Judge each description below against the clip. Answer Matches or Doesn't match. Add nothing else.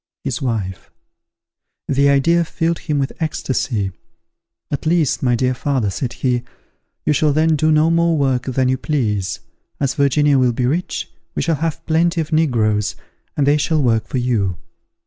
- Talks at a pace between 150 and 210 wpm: Matches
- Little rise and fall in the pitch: Doesn't match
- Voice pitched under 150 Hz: Matches